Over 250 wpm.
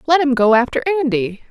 No: average, 200 wpm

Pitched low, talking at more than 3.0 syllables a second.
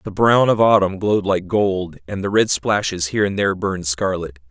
Yes: very low, 95 Hz; 5.6 syllables/s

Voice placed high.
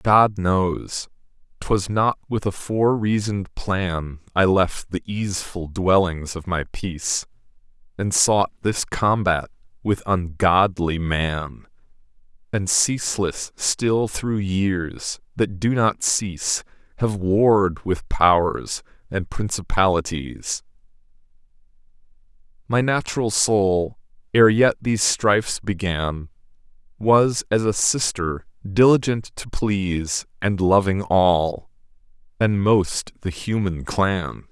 No: very low, 95 Hz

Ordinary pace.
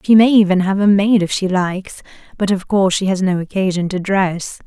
No: fast, 230 wpm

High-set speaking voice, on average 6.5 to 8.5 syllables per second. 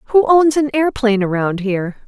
Yes: high, 240 Hz; 6.6 syllables/s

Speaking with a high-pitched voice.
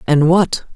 No: medium, 165 Hz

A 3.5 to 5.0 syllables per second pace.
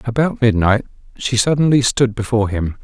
No: 5.5 syllables/s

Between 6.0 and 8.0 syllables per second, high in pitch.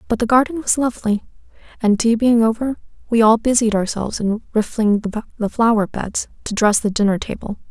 No: 5.6 syllables/s; high, 225 Hz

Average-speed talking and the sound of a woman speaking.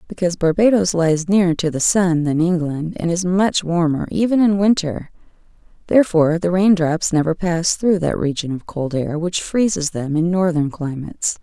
Yes: average, 180 wpm; female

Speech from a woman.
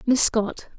Yes: female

